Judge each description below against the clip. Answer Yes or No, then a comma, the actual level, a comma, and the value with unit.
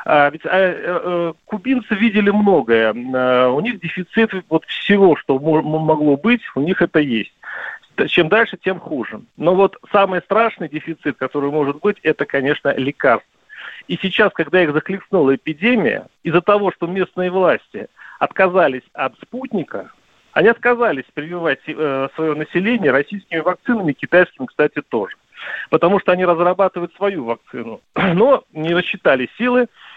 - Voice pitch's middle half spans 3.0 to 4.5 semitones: No, average, 5.2 semitones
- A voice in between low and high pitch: Yes, medium, 175 Hz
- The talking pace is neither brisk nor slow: Yes, average, 140 wpm